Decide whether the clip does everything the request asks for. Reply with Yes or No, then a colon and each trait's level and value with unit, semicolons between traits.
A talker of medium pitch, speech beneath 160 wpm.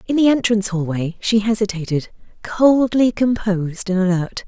No: high, 205 Hz; slow, 135 wpm